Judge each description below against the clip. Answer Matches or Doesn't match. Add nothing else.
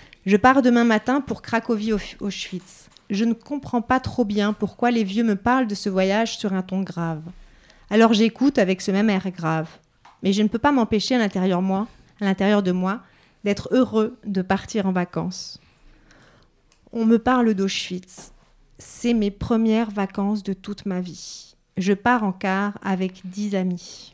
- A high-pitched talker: Matches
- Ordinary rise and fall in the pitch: Matches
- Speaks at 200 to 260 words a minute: Doesn't match